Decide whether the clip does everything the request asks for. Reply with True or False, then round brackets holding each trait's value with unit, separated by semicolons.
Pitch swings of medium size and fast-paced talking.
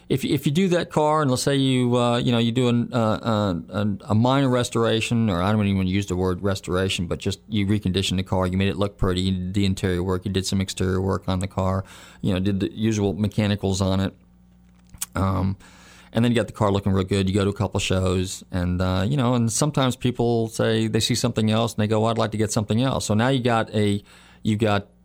True (3.4 semitones; 255 wpm)